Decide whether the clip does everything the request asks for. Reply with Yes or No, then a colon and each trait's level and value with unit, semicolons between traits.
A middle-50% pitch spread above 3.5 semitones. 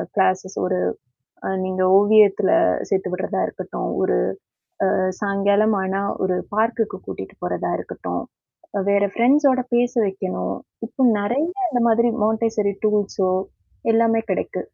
No: average, 3.0 semitones